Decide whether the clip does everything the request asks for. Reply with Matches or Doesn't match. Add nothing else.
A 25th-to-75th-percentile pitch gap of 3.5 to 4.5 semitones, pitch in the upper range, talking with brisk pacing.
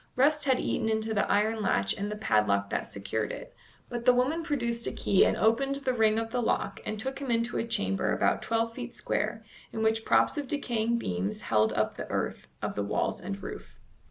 Matches